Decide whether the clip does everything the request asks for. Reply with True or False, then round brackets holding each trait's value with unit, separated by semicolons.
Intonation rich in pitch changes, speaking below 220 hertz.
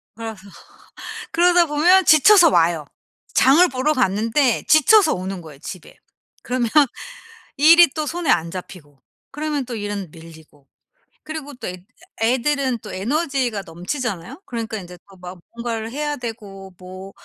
False (8.1 semitones; 235 Hz)